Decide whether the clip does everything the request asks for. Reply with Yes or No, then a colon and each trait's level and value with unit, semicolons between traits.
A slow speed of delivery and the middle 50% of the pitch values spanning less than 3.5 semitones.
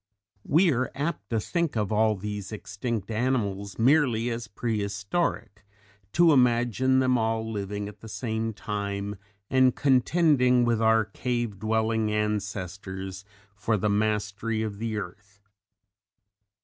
Yes: slow, 125 wpm; average, 3.1 semitones